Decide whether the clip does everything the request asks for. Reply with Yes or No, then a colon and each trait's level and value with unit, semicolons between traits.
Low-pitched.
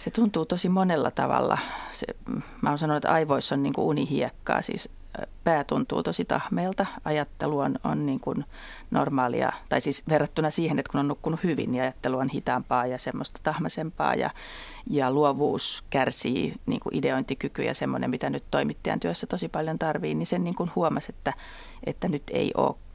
No: medium, 150 Hz